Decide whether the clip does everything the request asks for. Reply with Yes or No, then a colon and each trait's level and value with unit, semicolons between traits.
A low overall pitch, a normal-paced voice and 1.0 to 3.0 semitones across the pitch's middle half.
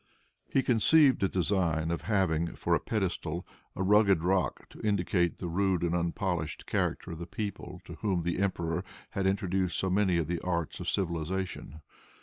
Yes: very low, 90 Hz; average, 170 wpm; narrow, 2.5 semitones